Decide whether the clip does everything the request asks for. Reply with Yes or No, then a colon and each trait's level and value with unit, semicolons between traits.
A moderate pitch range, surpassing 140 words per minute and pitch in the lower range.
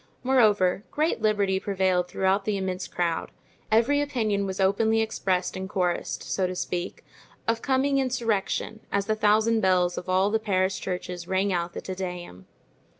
No: average, 3.1 semitones; average, 160 wpm; high, 195 Hz